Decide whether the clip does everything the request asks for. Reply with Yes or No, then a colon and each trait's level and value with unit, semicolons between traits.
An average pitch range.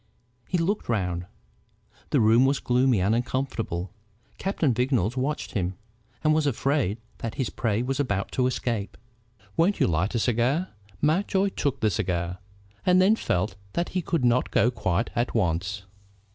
No: wide, 6.0 semitones